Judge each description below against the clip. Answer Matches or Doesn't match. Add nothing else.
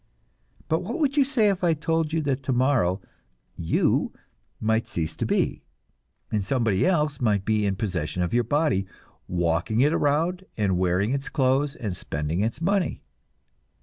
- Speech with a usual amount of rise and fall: Doesn't match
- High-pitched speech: Doesn't match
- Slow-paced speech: Doesn't match